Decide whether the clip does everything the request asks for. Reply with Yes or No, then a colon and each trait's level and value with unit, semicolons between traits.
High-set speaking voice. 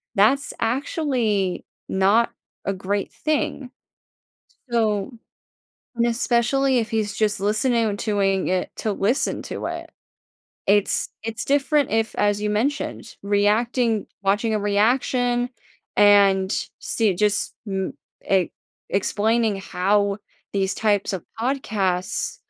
Yes: high, 210 Hz